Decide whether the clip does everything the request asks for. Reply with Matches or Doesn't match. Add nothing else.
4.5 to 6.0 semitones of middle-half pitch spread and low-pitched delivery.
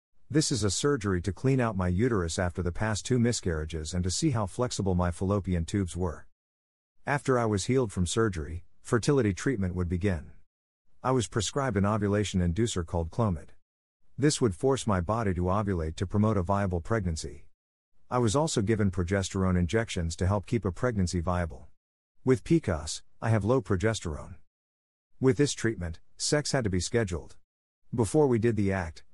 Matches